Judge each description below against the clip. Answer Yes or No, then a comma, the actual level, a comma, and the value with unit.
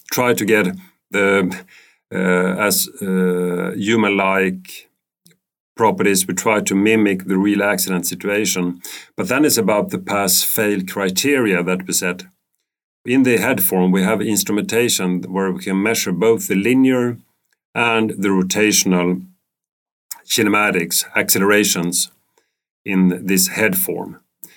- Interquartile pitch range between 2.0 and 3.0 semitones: Yes, narrow, 2.4 semitones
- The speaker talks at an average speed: No, slow, 120 wpm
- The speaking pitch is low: Yes, very low, 95 Hz